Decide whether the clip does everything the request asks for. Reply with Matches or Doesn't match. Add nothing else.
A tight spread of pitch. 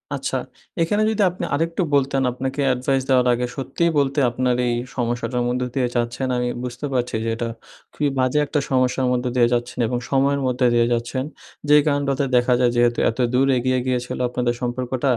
Matches